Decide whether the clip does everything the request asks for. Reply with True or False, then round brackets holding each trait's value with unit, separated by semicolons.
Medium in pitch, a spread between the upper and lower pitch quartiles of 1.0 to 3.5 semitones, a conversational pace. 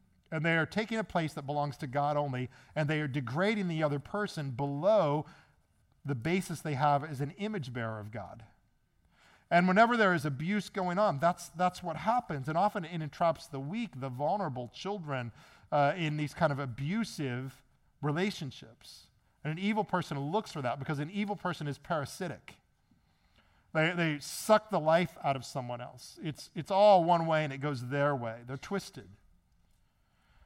False (150 Hz; 4.8 semitones; 175 wpm)